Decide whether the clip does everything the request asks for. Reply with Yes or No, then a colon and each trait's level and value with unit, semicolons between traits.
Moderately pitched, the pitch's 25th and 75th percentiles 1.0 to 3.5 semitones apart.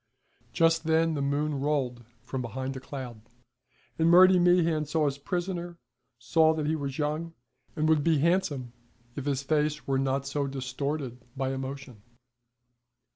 Yes: medium, 145 Hz; average, 3.2 semitones